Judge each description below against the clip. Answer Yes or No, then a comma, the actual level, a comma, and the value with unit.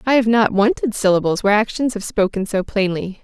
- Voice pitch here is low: No, high, 210 Hz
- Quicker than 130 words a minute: Yes, fast, 205 wpm